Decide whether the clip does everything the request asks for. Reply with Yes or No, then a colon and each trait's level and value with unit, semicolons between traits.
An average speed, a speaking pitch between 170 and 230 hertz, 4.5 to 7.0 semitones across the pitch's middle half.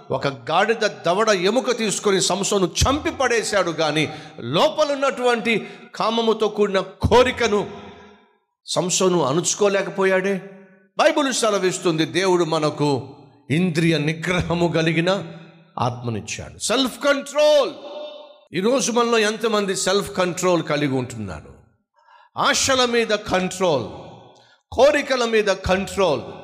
Yes: average, 85 wpm; high, 190 Hz; average, 5.2 semitones